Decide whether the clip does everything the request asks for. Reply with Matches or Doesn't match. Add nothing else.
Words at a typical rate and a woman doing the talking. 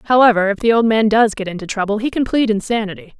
Doesn't match